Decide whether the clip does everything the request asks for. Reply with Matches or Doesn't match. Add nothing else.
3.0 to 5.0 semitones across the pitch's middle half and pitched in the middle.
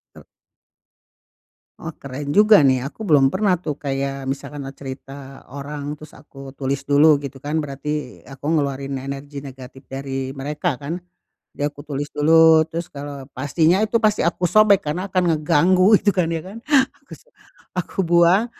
Matches